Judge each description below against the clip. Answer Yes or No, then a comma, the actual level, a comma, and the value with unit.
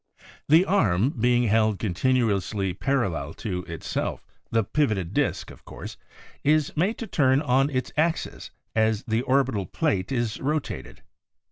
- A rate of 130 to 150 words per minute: Yes, average, 140 wpm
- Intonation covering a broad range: Yes, wide, 5.7 semitones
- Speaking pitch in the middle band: No, low, 120 Hz